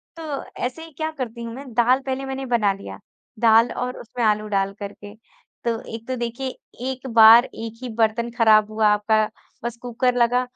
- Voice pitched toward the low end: No, high, 235 Hz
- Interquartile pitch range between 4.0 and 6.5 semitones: No, narrow, 2.6 semitones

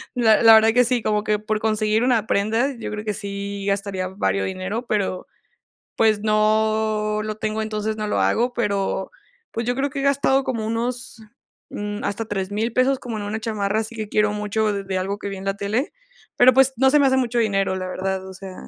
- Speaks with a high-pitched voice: Yes, high, 215 Hz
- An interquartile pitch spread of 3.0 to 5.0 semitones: No, narrow, 2.4 semitones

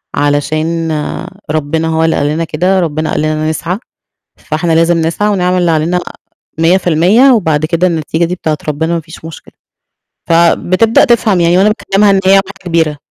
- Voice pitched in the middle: Yes, medium, 165 Hz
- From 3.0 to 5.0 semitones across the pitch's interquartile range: No, narrow, 2.6 semitones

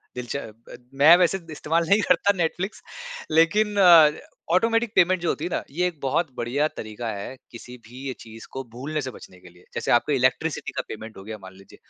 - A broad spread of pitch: Yes, wide, 6.8 semitones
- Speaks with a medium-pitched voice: Yes, medium, 145 Hz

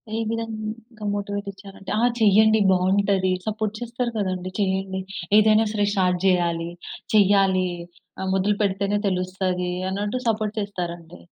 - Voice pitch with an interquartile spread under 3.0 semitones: Yes, narrow, 2.4 semitones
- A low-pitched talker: No, high, 200 Hz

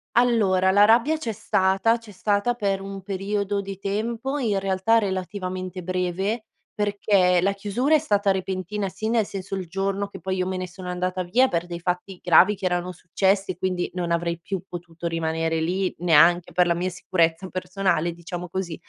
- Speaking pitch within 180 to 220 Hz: Yes, high, 190 Hz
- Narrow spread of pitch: Yes, narrow, 2.3 semitones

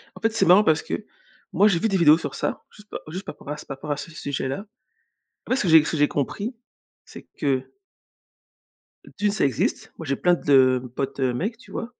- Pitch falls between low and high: Yes, medium, 160 Hz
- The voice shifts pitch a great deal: Yes, wide, 6.8 semitones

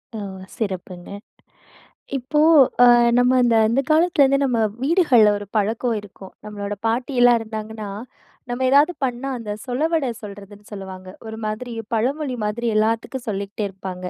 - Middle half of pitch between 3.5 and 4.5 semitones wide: Yes, average, 3.9 semitones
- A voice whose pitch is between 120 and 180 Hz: No, high, 225 Hz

